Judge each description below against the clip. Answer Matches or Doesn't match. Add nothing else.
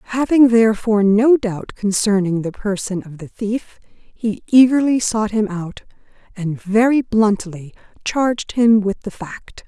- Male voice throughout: Doesn't match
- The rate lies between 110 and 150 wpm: Matches